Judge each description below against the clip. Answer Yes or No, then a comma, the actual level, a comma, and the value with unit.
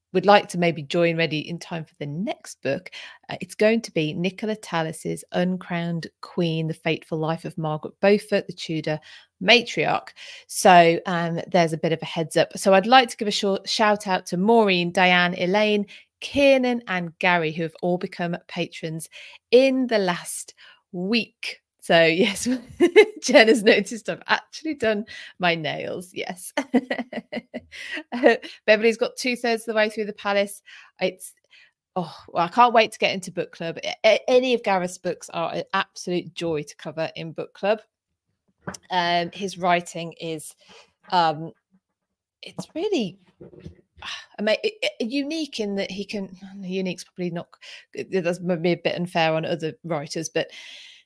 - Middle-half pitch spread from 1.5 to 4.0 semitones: No, average, 5.1 semitones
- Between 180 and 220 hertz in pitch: Yes, high, 190 Hz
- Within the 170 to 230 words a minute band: No, average, 160 wpm